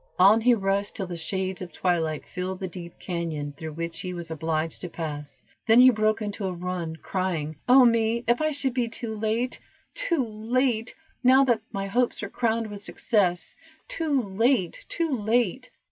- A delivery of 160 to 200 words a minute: Yes, average, 180 wpm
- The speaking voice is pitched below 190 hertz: No, high, 205 Hz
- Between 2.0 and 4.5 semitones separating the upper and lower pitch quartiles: No, average, 5.3 semitones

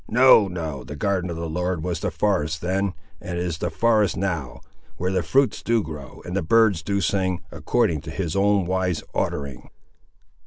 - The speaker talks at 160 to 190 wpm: Yes, average, 185 wpm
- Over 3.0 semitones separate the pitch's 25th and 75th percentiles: Yes, average, 3.5 semitones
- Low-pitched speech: Yes, very low, 90 Hz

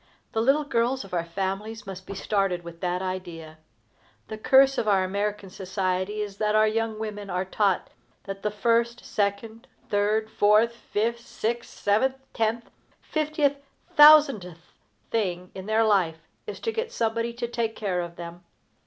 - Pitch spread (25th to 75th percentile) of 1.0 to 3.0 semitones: No, average, 3.6 semitones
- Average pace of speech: Yes, average, 160 wpm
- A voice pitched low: No, high, 210 Hz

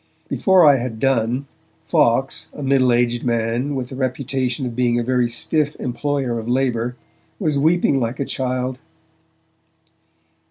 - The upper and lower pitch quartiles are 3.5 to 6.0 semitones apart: No, narrow, 2.4 semitones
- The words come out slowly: No, average, 145 wpm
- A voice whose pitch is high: No, low, 130 Hz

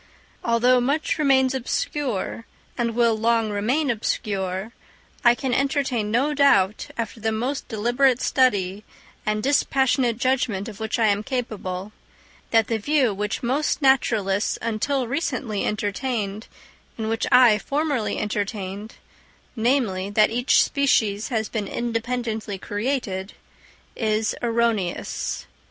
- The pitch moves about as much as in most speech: Yes, average, 3.5 semitones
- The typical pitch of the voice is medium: No, high, 230 Hz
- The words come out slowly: Yes, slow, 115 wpm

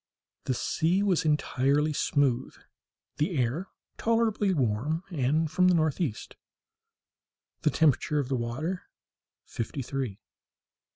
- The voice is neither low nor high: Yes, medium, 150 Hz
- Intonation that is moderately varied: Yes, average, 4.7 semitones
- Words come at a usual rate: No, slow, 110 wpm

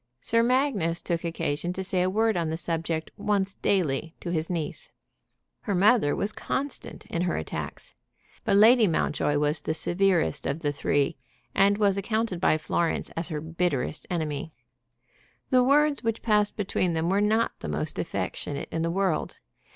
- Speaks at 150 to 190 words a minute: Yes, average, 165 wpm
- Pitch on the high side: No, medium, 180 Hz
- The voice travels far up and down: No, average, 4.6 semitones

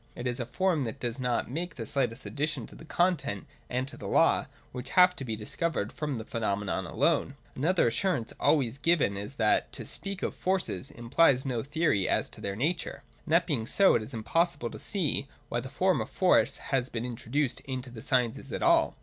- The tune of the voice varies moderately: No, wide, 5.8 semitones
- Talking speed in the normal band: No, fast, 210 wpm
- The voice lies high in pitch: No, low, 130 Hz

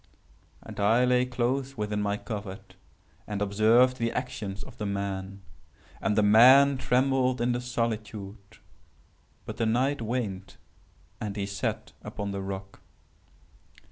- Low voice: Yes, low, 110 Hz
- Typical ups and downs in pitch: Yes, average, 3.9 semitones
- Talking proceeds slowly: Yes, slow, 130 wpm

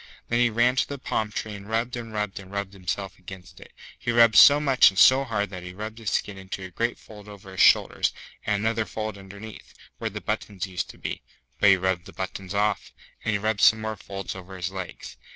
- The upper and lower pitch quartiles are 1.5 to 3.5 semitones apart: Yes, narrow, 2.6 semitones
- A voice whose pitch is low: Yes, low, 100 Hz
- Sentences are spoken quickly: Yes, fast, 235 wpm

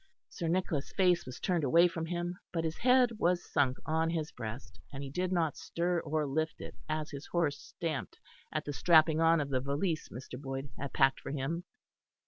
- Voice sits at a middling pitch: Yes, medium, 160 Hz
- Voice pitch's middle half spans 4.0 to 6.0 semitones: No, average, 3.6 semitones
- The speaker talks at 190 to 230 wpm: Yes, average, 200 wpm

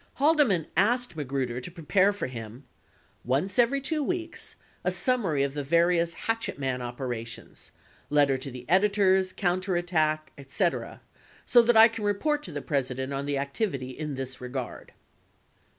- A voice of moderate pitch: Yes, medium, 160 Hz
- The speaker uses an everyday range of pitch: No, wide, 7.3 semitones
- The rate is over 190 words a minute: No, average, 150 wpm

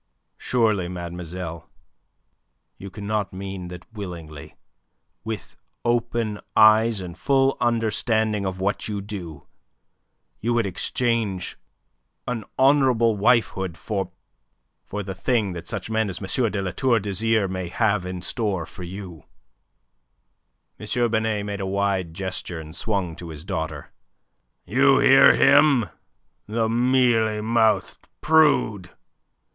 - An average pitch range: Yes, average, 3.7 semitones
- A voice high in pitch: No, low, 105 Hz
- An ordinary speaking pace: No, slow, 125 wpm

